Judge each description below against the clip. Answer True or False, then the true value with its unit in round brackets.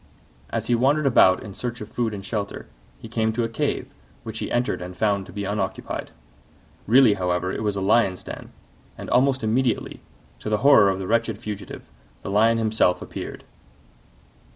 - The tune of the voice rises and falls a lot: False (3.1 semitones)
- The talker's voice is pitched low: True (110 Hz)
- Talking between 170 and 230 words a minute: True (180 wpm)